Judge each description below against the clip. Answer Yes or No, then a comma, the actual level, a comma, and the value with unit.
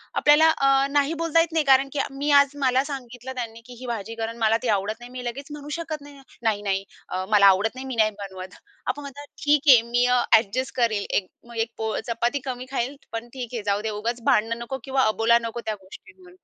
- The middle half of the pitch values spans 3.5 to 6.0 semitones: Yes, average, 3.8 semitones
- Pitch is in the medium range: No, high, 245 Hz